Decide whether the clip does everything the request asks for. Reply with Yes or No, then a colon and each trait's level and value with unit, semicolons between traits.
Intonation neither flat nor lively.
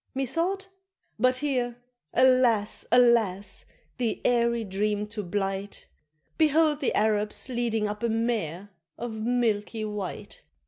Yes: average, 3.2 semitones